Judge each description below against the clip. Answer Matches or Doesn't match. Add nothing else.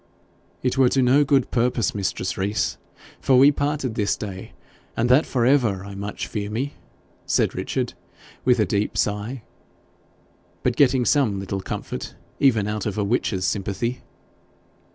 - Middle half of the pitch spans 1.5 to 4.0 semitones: Doesn't match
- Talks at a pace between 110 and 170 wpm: Matches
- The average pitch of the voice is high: Doesn't match